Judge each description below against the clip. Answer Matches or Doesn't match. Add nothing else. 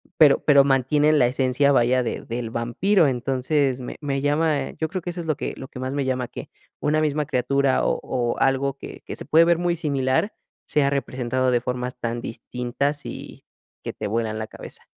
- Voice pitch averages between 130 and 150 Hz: Matches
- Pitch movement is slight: Doesn't match